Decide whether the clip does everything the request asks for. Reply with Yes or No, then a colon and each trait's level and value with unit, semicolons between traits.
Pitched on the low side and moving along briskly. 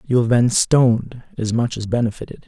No: low, 120 Hz; average, 195 wpm